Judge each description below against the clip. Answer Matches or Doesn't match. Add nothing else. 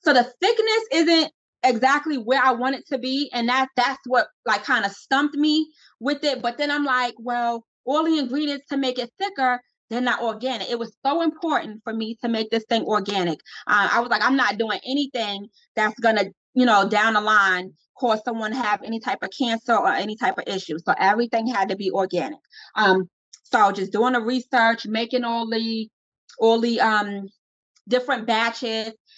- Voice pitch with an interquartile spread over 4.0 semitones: Doesn't match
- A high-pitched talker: Matches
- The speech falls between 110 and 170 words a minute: Doesn't match